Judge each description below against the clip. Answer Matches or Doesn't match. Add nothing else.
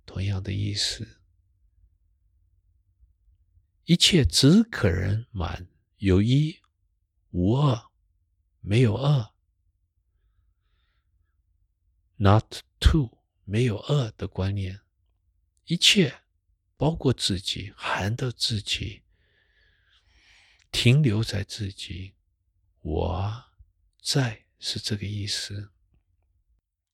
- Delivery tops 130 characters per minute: Doesn't match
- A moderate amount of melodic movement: Matches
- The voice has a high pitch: Doesn't match